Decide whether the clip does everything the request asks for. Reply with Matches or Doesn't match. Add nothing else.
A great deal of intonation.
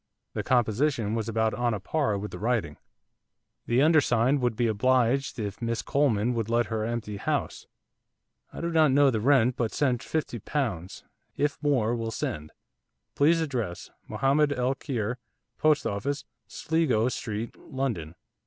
Doesn't match